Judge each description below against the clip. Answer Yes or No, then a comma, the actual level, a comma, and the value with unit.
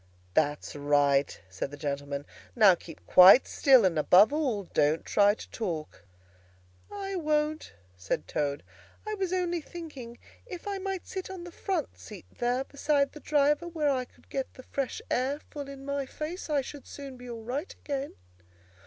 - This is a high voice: Yes, very high, 270 Hz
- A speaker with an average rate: Yes, average, 170 wpm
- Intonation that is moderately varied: No, wide, 9.0 semitones